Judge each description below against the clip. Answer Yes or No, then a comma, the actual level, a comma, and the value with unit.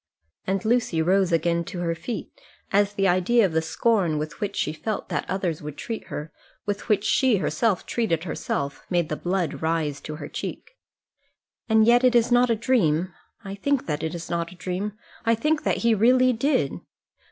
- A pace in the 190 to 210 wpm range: Yes, average, 195 wpm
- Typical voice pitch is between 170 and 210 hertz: Yes, high, 190 Hz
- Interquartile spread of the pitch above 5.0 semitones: Yes, wide, 5.6 semitones